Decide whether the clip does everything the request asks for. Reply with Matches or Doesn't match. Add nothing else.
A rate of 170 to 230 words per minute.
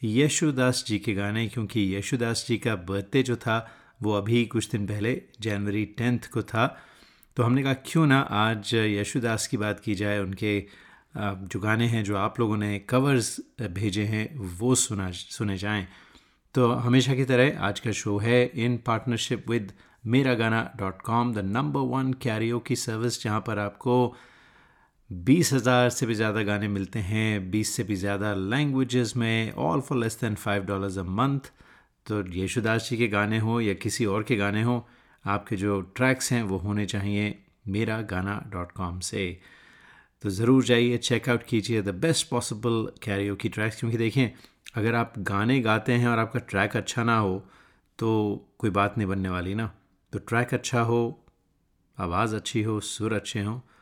Matches